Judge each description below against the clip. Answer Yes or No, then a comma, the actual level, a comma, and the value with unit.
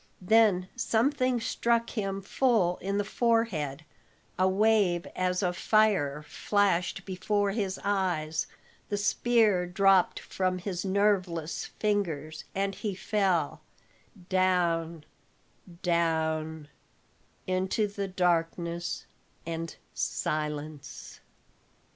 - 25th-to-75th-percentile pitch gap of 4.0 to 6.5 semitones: No, average, 3.5 semitones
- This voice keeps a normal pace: No, slow, 90 wpm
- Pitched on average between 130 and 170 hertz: No, medium, 185 Hz